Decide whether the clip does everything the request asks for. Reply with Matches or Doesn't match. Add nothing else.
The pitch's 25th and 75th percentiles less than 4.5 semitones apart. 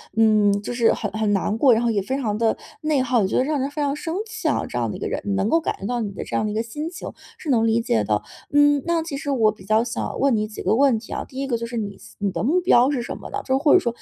Doesn't match